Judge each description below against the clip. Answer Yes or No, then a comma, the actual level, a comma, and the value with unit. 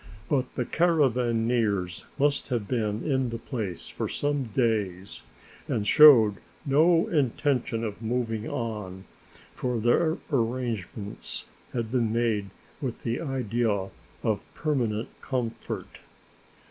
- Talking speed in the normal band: No, slow, 110 wpm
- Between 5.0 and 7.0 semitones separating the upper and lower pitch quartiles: No, average, 3.6 semitones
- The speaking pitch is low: Yes, low, 115 Hz